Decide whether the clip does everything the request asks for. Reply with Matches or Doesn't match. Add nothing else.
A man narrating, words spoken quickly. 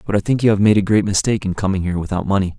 Matches